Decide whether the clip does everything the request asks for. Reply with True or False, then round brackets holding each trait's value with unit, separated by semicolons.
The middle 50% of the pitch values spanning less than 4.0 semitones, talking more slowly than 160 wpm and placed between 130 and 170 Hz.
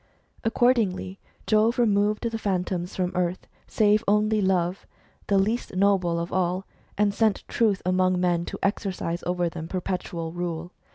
False (2.9 semitones; 145 wpm; 185 Hz)